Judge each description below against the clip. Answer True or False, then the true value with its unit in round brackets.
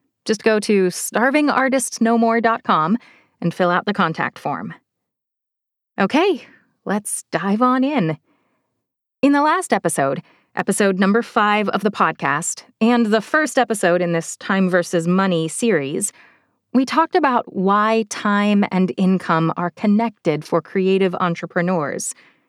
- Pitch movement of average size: True (5.0 semitones)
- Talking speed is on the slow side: True (125 wpm)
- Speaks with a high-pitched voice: True (205 Hz)